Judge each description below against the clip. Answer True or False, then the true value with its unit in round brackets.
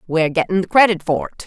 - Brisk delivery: True (245 wpm)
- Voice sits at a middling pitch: True (165 Hz)